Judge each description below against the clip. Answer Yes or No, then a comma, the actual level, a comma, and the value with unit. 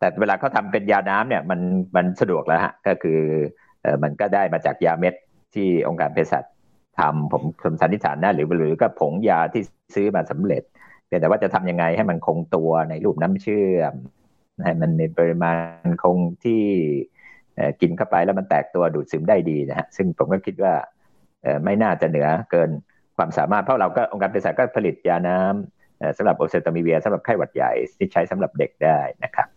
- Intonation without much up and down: Yes, narrow, 2.2 semitones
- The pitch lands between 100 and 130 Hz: No, very low, 85 Hz